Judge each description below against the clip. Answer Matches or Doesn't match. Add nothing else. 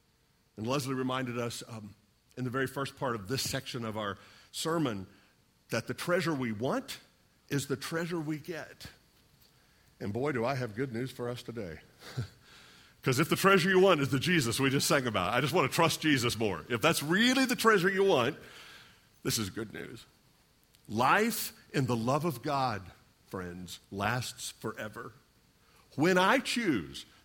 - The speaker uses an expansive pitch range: Matches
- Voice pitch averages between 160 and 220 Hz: Doesn't match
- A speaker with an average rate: Matches